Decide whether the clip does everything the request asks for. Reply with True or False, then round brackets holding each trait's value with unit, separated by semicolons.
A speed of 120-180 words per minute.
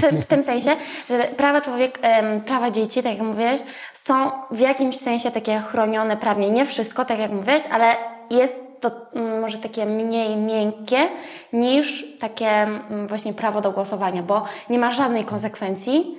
True (150 wpm)